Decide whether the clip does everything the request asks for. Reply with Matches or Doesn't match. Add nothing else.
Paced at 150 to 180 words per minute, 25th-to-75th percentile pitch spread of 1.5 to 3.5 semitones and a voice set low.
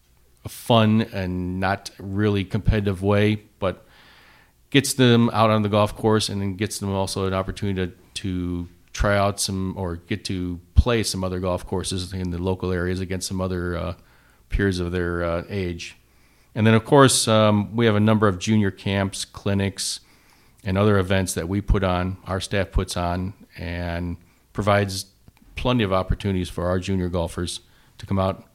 Matches